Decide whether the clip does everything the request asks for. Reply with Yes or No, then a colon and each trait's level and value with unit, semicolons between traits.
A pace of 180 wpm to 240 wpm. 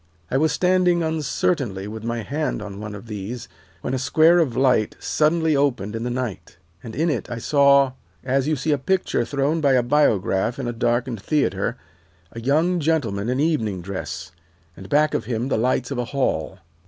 Yes: average, 190 wpm